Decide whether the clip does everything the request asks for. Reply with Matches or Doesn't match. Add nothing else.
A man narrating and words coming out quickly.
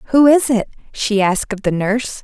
Doesn't match